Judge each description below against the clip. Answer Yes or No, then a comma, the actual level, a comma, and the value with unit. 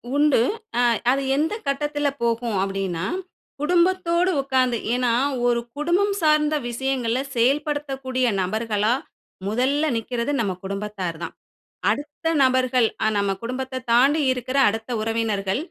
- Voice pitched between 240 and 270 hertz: Yes, very high, 255 Hz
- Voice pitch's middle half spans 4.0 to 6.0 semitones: Yes, average, 4.5 semitones